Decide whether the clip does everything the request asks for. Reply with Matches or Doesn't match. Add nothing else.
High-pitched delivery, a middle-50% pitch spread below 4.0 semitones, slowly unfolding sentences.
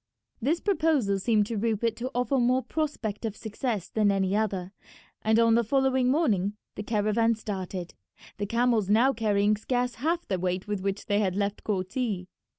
Doesn't match